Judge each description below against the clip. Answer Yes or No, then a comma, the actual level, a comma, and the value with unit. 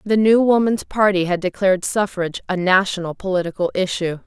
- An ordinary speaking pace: Yes, average, 155 wpm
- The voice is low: No, high, 190 Hz